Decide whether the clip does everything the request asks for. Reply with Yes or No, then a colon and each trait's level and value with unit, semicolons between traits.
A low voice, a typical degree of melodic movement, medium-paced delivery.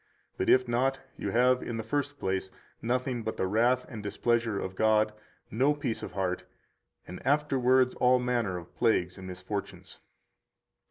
Yes: low, 120 Hz; average, 4.0 semitones; average, 160 wpm